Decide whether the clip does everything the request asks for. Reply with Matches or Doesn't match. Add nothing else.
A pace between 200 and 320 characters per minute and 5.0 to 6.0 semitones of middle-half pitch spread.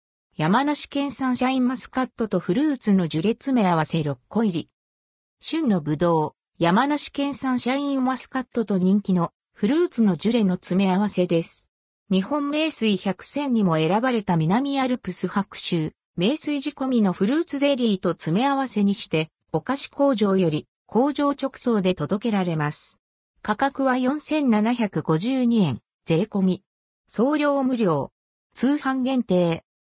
Doesn't match